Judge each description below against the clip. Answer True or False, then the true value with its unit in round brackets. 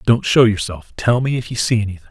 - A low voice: True (110 Hz)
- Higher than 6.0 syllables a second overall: True (6.3 syllables/s)